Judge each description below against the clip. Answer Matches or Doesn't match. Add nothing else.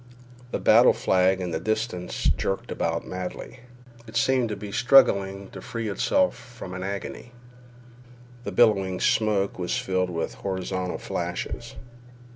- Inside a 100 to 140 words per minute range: Matches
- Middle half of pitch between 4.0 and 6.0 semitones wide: Doesn't match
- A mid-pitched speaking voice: Doesn't match